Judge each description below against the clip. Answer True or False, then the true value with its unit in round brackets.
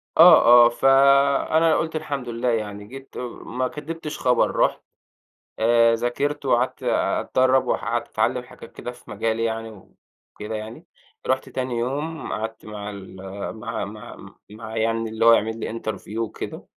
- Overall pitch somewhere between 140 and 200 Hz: False (120 Hz)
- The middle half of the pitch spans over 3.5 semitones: False (3.2 semitones)